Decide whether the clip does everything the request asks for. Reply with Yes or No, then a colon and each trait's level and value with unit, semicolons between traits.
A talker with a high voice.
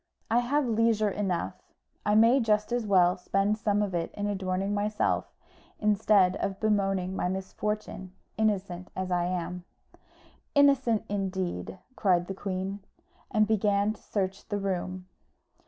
Yes: high, 200 Hz